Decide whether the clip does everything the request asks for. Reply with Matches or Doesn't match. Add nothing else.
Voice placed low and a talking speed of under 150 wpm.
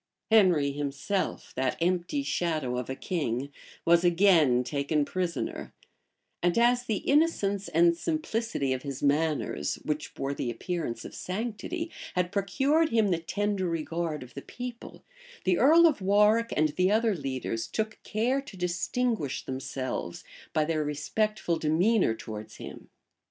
Doesn't match